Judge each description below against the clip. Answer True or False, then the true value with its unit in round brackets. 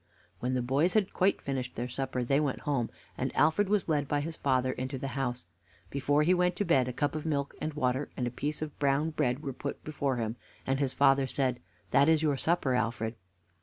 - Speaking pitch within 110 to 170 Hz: True (140 Hz)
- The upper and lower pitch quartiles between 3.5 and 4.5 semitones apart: False (3.1 semitones)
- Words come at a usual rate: False (225 wpm)